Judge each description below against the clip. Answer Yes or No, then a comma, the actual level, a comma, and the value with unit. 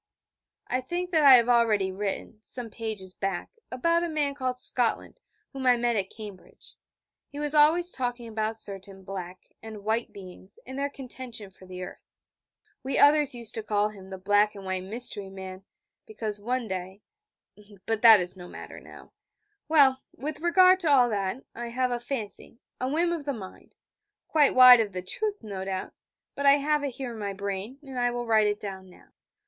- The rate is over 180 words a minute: Yes, average, 190 wpm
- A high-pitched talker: Yes, high, 230 Hz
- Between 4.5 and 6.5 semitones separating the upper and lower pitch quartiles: Yes, average, 5.3 semitones